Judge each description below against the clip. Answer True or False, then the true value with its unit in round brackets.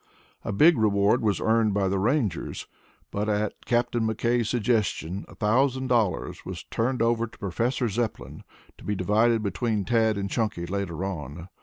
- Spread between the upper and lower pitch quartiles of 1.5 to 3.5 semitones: True (3.1 semitones)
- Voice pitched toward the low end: True (110 Hz)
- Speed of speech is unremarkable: True (160 wpm)